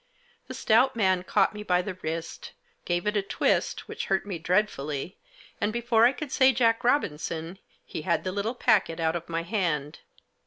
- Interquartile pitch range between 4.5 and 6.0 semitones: Yes, average, 5.0 semitones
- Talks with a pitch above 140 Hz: Yes, high, 190 Hz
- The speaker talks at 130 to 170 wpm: No, average, 185 wpm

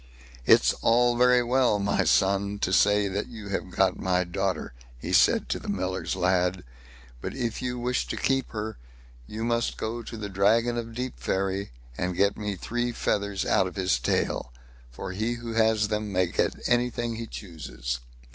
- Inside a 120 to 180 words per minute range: Yes, average, 175 wpm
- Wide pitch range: No, average, 3.9 semitones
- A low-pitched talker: Yes, low, 105 Hz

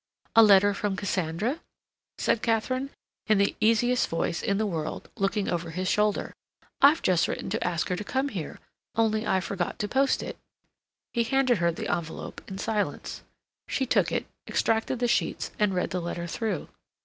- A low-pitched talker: No, high, 205 Hz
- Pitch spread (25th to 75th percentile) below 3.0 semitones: No, average, 4.1 semitones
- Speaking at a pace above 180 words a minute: No, average, 175 wpm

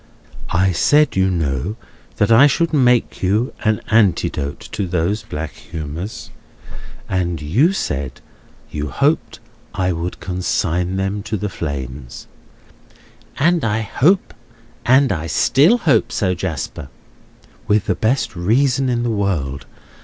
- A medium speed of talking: No, slow, 120 wpm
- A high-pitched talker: No, low, 100 Hz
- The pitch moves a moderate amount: No, wide, 6.4 semitones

